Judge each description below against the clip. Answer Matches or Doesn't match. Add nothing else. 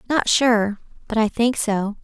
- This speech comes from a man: Doesn't match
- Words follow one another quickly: Doesn't match